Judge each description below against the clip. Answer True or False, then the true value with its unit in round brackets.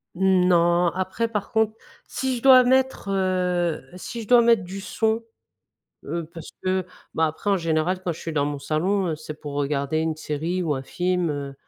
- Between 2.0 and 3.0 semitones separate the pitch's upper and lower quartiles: False (4.2 semitones)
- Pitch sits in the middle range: True (180 Hz)